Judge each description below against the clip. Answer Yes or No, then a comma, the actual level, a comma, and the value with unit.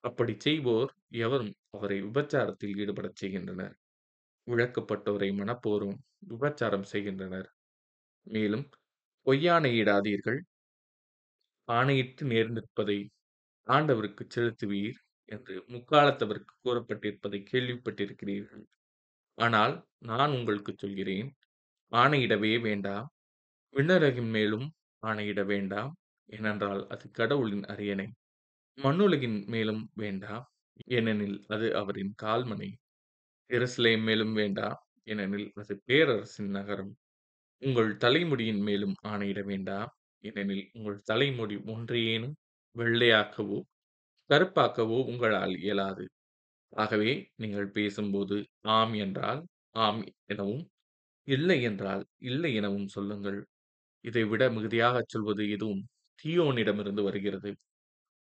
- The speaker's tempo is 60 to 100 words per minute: Yes, average, 85 wpm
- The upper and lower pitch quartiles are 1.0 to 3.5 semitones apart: Yes, average, 3.1 semitones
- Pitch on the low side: Yes, low, 105 Hz